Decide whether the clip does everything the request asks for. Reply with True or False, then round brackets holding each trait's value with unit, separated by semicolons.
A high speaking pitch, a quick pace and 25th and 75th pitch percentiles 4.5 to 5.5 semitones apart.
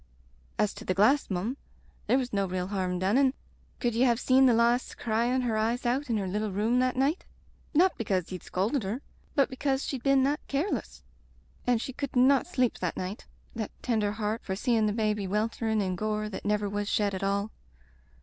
False (225 Hz; 210 wpm; 4.0 semitones)